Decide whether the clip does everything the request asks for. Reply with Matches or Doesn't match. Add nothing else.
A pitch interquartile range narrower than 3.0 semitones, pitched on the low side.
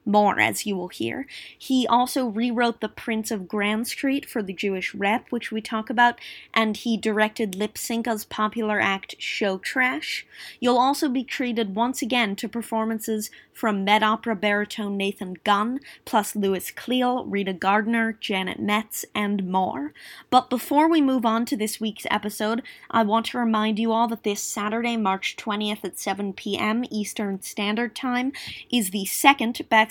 Doesn't match